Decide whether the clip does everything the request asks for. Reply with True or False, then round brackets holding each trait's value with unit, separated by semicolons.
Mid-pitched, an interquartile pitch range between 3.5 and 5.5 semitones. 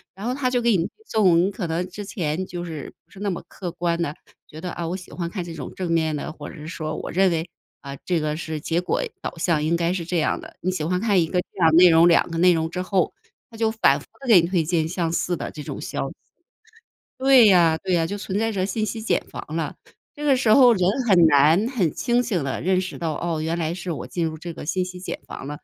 False (175 Hz; 3.0 semitones)